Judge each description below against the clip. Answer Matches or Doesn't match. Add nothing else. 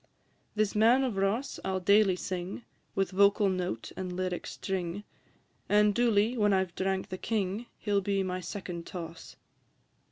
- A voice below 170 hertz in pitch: Doesn't match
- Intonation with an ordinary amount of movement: Doesn't match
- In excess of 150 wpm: Matches